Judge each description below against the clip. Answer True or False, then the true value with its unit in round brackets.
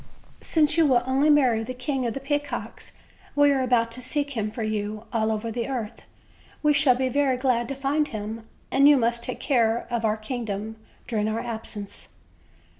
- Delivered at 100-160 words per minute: False (190 wpm)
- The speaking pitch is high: True (245 Hz)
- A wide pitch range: False (3.7 semitones)